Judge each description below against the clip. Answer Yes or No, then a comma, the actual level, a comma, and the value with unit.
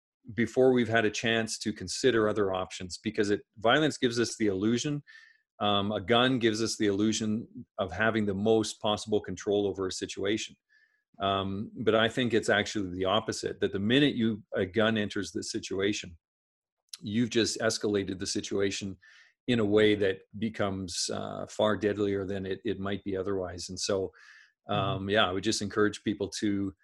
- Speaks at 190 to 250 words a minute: No, average, 175 wpm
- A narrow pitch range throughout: Yes, narrow, 2.3 semitones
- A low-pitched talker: Yes, low, 105 Hz